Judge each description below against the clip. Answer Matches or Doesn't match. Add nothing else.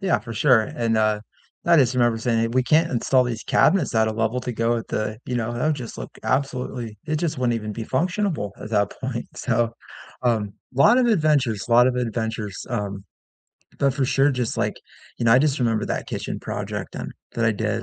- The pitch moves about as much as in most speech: Matches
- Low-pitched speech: Matches